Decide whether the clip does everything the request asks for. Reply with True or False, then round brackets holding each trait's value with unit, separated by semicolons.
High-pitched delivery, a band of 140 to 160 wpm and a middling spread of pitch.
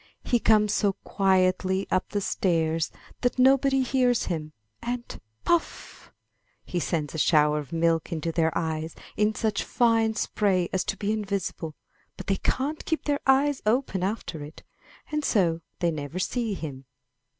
False (195 Hz; 155 wpm; 6.4 semitones)